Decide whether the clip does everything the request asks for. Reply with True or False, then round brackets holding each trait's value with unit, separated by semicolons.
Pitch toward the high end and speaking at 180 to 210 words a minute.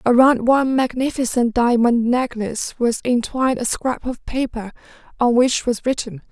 False (245 Hz; 145 wpm)